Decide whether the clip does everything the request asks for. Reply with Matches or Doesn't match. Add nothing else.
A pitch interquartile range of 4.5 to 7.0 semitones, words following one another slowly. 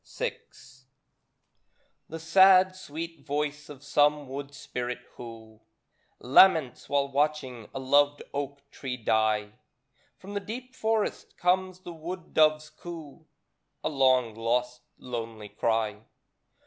Matches